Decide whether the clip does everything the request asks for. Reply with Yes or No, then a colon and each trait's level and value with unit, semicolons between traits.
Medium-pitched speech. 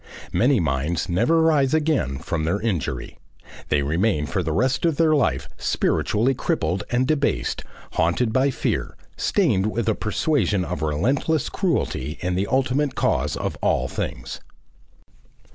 No: low, 110 Hz